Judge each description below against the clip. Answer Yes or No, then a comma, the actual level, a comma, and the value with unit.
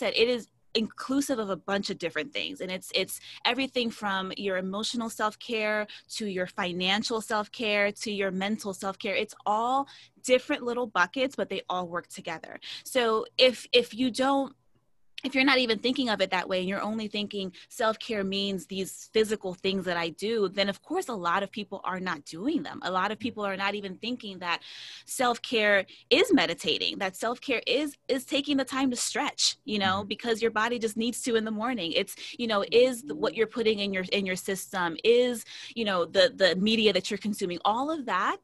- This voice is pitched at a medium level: No, high, 215 Hz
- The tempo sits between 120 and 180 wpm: No, average, 200 wpm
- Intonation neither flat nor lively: Yes, average, 4.0 semitones